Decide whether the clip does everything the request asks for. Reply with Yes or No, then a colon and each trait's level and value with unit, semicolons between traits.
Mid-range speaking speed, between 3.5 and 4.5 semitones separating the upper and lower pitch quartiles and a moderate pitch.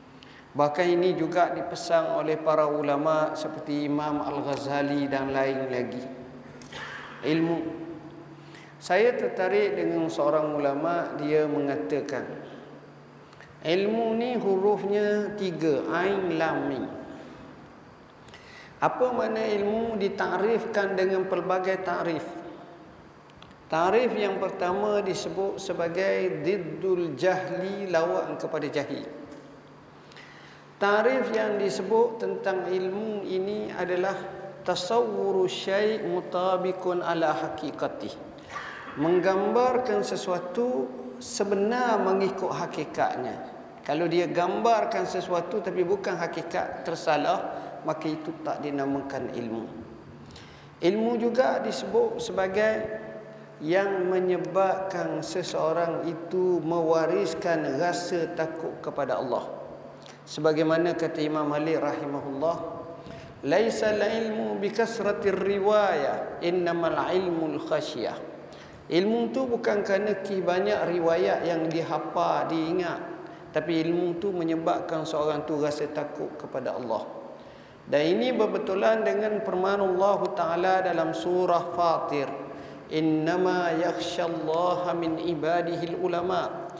Yes: average, 95 wpm; average, 3.8 semitones; medium, 175 Hz